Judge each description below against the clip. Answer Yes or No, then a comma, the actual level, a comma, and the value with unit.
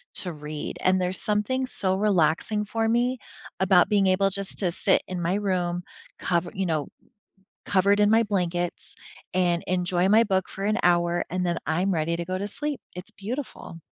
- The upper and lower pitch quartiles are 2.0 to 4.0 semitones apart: Yes, average, 2.8 semitones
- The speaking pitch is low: No, medium, 185 Hz